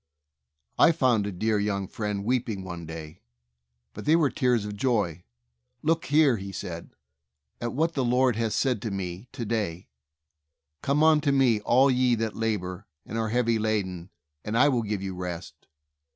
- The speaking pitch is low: Yes, low, 110 Hz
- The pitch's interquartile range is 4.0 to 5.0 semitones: Yes, average, 4.7 semitones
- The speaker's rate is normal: Yes, average, 170 wpm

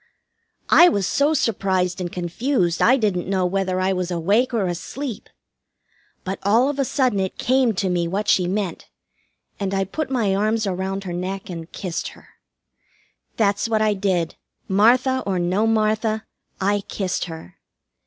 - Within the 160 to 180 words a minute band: Yes, average, 165 wpm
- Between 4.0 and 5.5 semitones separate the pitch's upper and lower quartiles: No, average, 3.4 semitones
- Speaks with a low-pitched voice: No, high, 195 Hz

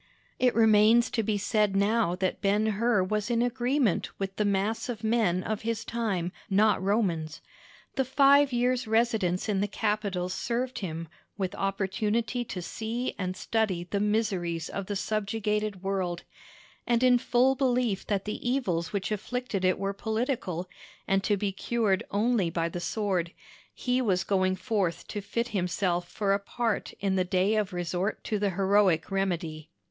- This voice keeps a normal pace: Yes, average, 165 wpm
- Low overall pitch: No, high, 205 Hz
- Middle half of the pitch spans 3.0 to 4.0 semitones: Yes, average, 3.5 semitones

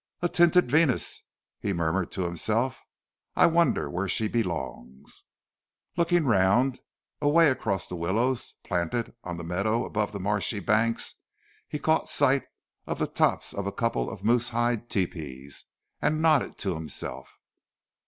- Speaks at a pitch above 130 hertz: No, low, 110 Hz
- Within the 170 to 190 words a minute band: No, average, 145 wpm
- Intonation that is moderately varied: No, wide, 6.7 semitones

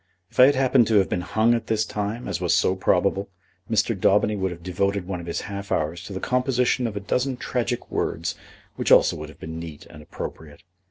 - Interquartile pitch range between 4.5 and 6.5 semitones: Yes, average, 5.0 semitones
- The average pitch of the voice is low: Yes, low, 100 Hz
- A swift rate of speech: Yes, fast, 225 wpm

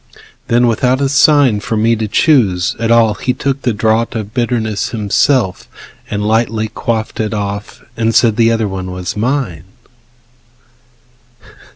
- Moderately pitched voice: No, low, 115 Hz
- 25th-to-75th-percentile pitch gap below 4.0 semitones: Yes, narrow, 2.6 semitones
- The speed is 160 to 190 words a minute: No, average, 150 wpm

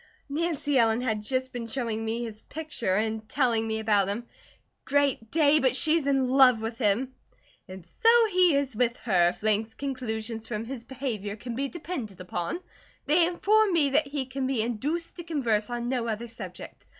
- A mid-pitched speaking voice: No, high, 245 Hz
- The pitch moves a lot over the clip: No, average, 4.2 semitones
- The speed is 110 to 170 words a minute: No, average, 185 wpm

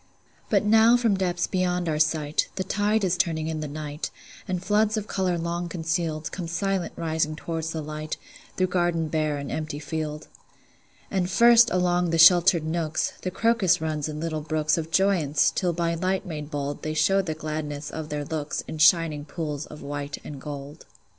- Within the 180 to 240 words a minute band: Yes, average, 185 wpm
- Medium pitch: Yes, medium, 165 Hz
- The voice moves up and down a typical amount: Yes, average, 3.0 semitones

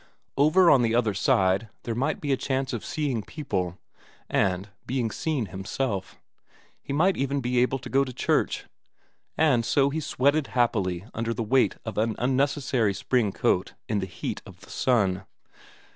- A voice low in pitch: Yes, low, 125 Hz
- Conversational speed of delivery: Yes, average, 170 wpm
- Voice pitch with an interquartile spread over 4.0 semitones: Yes, average, 4.9 semitones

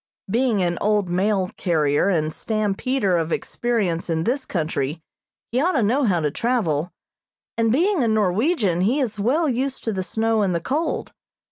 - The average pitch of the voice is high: Yes, high, 210 Hz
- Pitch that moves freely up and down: Yes, wide, 5.8 semitones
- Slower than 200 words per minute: Yes, average, 170 wpm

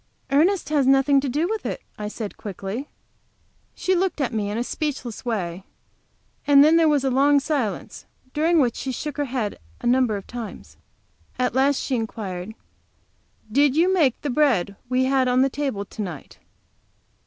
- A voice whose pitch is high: Yes, very high, 265 Hz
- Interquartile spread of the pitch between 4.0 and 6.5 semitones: Yes, average, 4.8 semitones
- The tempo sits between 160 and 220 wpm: Yes, average, 175 wpm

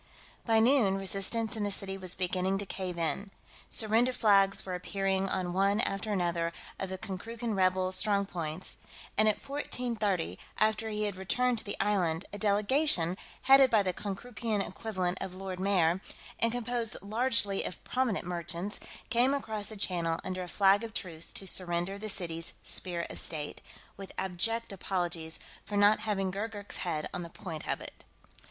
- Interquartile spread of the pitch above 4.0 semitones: No, average, 3.1 semitones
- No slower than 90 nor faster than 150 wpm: No, average, 170 wpm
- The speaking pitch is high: Yes, high, 195 Hz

